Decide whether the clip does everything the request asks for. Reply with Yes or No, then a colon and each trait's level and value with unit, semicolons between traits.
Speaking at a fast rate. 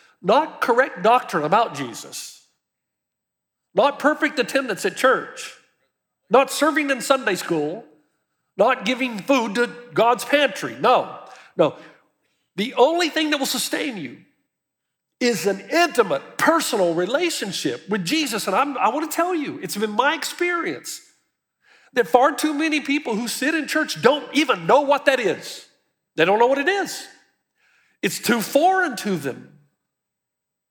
No: average, 145 wpm